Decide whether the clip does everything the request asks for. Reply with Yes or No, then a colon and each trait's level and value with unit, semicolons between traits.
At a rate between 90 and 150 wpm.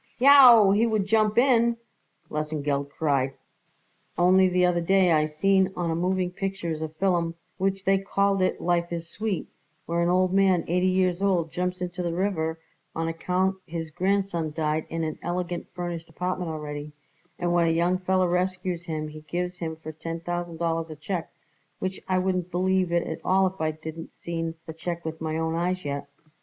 No: average, 185 wpm